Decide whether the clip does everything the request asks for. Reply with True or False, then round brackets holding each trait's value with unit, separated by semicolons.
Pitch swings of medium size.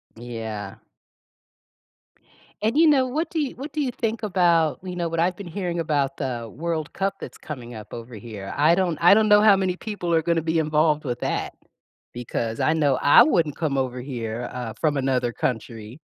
False (7.1 semitones)